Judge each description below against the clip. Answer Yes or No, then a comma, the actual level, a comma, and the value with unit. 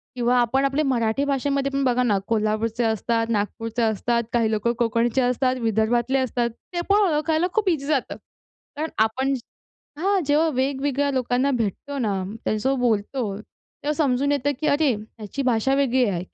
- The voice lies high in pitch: Yes, very high, 250 Hz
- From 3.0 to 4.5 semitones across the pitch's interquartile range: Yes, average, 3.6 semitones